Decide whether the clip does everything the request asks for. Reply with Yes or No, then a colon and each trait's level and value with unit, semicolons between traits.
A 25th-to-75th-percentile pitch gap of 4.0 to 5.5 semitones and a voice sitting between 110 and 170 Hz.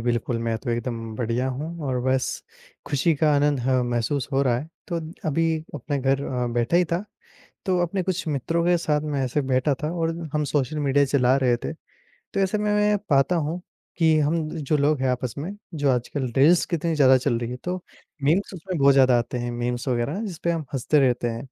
Yes: average, 4.5 semitones; medium, 140 Hz